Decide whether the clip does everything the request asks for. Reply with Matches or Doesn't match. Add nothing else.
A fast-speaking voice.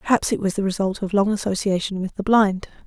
Matches